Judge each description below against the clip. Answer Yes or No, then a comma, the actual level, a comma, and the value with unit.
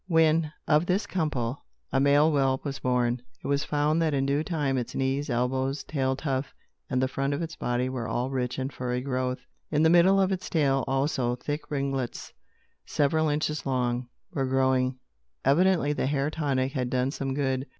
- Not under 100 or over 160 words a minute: No, average, 185 wpm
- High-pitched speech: No, low, 135 Hz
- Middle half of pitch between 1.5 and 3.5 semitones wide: Yes, average, 2.7 semitones